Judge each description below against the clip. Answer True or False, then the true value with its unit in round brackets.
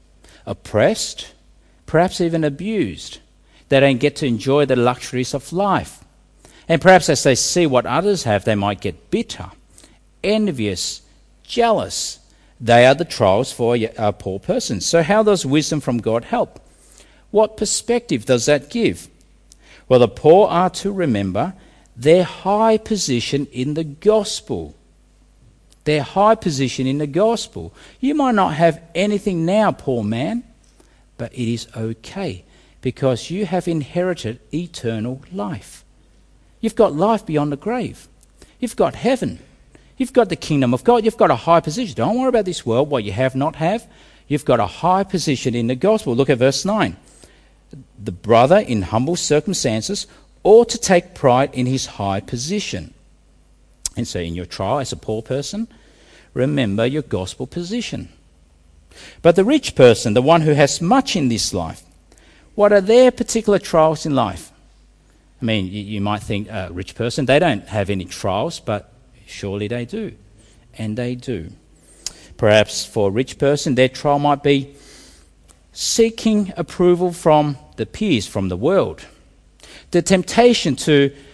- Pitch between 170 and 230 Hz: False (140 Hz)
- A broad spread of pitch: True (8.5 semitones)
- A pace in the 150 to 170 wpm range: True (155 wpm)